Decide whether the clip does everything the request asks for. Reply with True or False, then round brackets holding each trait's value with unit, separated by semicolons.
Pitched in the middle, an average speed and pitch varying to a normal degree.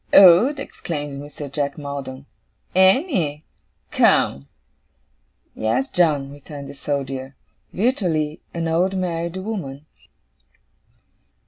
False (155 Hz; 90 wpm; 4.7 semitones)